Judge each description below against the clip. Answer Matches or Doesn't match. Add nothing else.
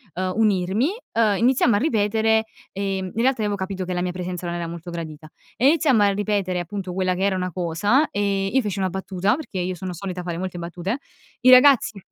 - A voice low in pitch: Doesn't match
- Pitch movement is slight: Doesn't match